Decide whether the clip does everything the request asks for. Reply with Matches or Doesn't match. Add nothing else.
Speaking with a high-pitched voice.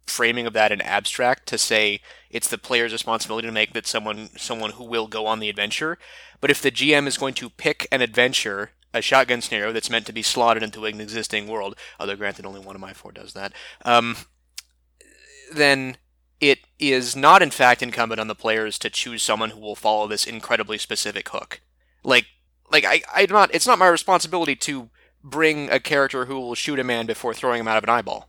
Doesn't match